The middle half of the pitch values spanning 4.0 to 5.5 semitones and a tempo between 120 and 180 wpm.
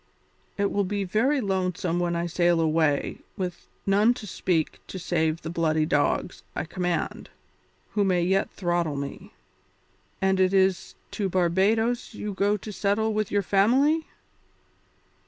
No: average, 3.0 semitones; average, 145 wpm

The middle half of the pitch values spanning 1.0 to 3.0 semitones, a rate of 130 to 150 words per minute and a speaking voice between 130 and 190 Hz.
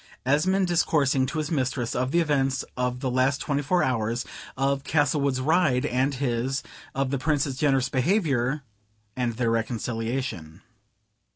Yes: average, 2.7 semitones; average, 145 wpm; low, 135 Hz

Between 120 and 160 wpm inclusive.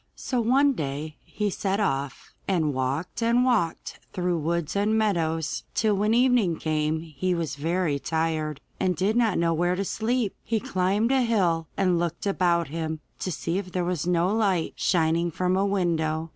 No: average, 175 wpm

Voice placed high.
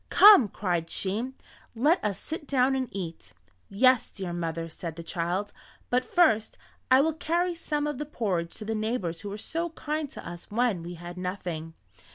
Yes: high, 210 Hz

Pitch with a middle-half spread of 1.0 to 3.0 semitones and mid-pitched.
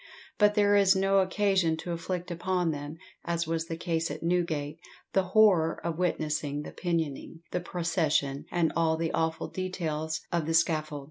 Yes: narrow, 2.4 semitones; medium, 165 Hz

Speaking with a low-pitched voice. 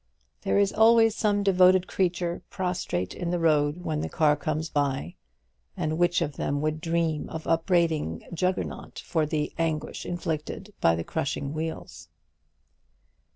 No: medium, 160 Hz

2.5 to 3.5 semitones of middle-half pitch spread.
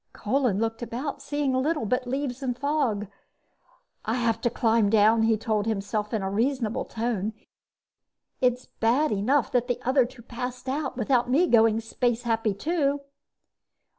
Yes: average, 2.9 semitones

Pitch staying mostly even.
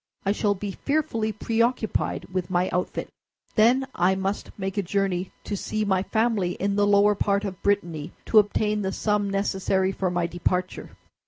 Yes: narrow, 2.2 semitones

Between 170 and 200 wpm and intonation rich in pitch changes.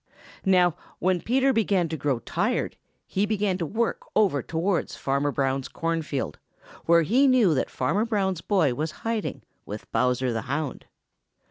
No: average, 155 wpm; wide, 6.6 semitones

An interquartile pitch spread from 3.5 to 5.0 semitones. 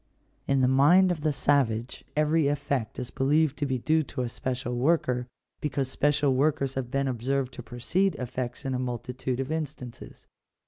No: average, 2.7 semitones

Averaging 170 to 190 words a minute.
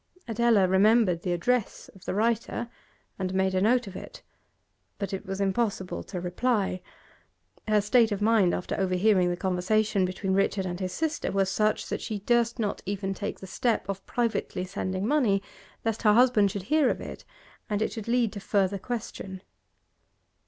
Yes: average, 175 wpm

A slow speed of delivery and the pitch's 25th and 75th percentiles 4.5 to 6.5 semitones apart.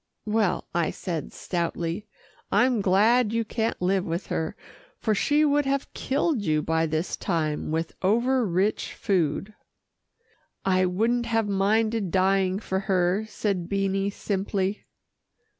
No: slow, 130 wpm; average, 3.7 semitones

